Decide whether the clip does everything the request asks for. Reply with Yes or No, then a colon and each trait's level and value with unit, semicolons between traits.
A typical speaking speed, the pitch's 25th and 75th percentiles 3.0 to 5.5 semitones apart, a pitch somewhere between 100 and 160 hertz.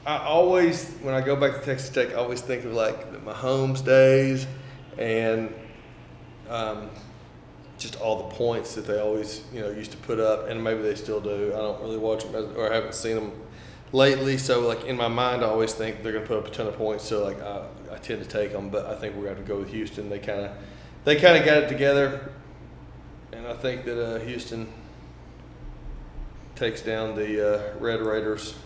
No: fast, 215 wpm; average, 3.3 semitones; low, 110 Hz